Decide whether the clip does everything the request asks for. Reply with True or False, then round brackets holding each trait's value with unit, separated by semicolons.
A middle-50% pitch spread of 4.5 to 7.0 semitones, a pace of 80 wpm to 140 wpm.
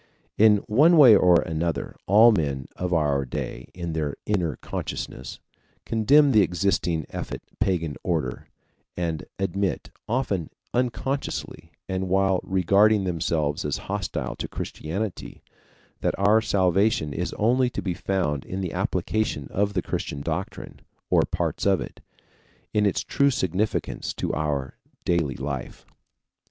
True (4.8 semitones; 135 wpm)